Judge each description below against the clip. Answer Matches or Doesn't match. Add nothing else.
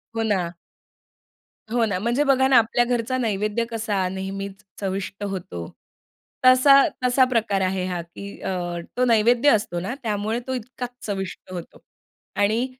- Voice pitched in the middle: Doesn't match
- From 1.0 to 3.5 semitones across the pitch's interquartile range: Doesn't match